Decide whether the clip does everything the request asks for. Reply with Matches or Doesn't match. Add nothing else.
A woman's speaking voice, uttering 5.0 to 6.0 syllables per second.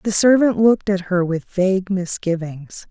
Doesn't match